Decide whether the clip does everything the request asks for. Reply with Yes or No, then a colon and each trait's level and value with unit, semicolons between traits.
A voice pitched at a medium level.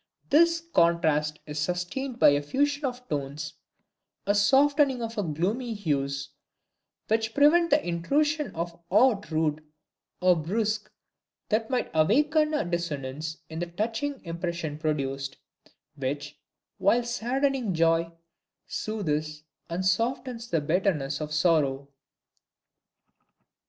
Yes: medium, 180 Hz